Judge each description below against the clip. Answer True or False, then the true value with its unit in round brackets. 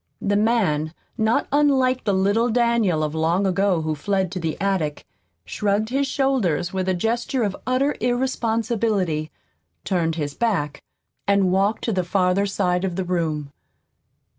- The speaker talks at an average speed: True (150 wpm)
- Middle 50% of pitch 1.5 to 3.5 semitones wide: False (5.0 semitones)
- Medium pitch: False (195 Hz)